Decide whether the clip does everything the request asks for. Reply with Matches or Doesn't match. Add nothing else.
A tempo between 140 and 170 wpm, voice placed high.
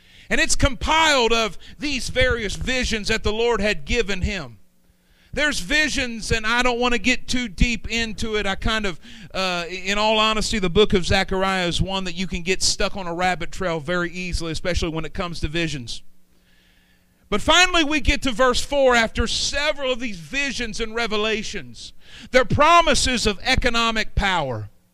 Doesn't match